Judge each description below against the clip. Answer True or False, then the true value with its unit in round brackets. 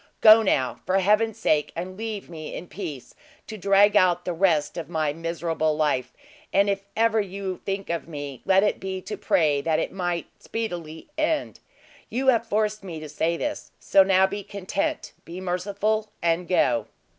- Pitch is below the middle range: False (185 Hz)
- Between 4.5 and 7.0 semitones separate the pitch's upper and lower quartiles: False (3.8 semitones)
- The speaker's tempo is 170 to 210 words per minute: True (180 wpm)